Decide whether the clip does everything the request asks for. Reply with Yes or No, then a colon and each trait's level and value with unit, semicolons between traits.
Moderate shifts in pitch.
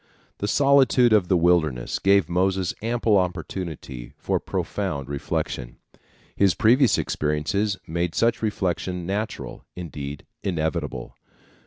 Yes: average, 5.0 semitones